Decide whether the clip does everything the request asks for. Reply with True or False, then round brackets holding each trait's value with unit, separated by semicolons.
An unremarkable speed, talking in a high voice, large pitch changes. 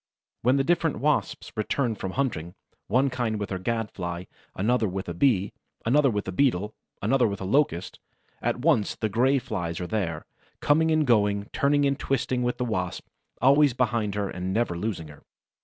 False (185 wpm; 115 Hz; 6.1 semitones)